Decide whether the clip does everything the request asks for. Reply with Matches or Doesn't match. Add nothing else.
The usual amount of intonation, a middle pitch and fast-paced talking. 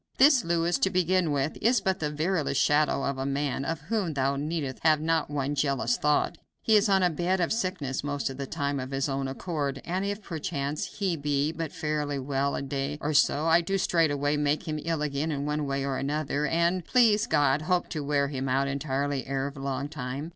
Matches